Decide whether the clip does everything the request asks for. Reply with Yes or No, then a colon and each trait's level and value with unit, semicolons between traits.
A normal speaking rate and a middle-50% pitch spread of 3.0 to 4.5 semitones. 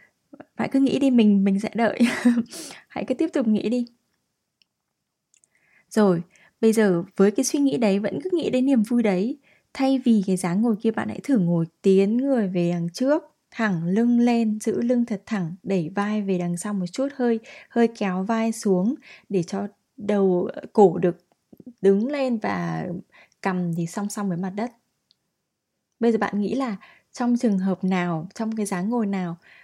Yes: average, 185 wpm; average, 4.0 semitones